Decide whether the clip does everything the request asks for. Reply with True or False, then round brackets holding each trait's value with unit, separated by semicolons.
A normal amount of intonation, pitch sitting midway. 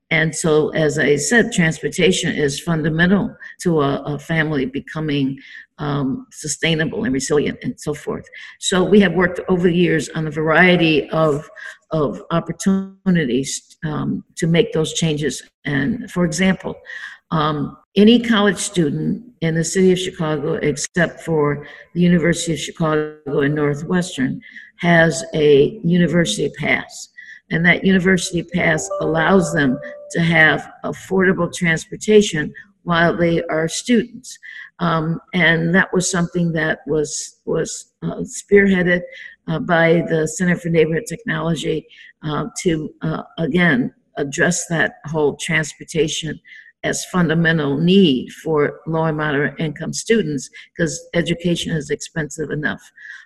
True (3.0 semitones; 165 Hz)